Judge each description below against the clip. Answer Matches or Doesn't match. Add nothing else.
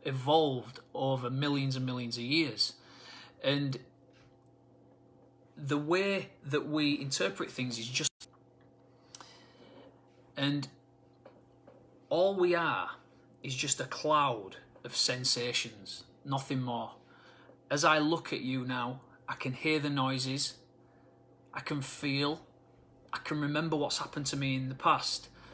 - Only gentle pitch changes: Matches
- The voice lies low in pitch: Matches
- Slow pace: Matches